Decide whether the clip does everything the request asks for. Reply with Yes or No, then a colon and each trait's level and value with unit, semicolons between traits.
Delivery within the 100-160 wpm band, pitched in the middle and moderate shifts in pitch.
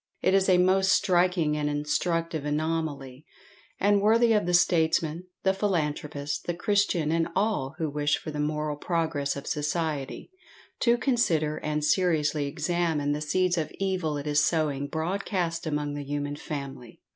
Yes: average, 155 wpm; medium, 160 Hz; average, 3.4 semitones